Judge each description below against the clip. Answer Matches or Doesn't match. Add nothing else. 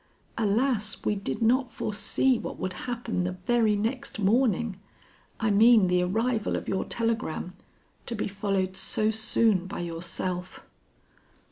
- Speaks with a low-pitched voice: Doesn't match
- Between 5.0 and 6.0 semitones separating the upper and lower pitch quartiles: Doesn't match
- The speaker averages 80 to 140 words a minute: Matches